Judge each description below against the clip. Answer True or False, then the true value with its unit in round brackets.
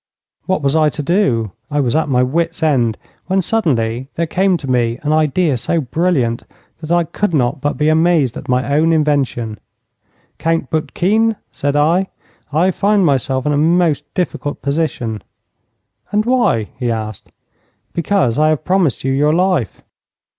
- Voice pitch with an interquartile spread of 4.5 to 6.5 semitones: True (4.9 semitones)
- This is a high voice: False (150 Hz)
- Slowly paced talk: False (160 wpm)